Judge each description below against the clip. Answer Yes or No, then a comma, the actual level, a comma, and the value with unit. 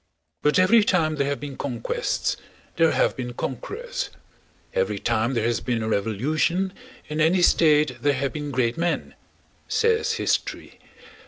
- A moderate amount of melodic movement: No, wide, 6.1 semitones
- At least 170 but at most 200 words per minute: No, average, 150 wpm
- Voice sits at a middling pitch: Yes, medium, 150 Hz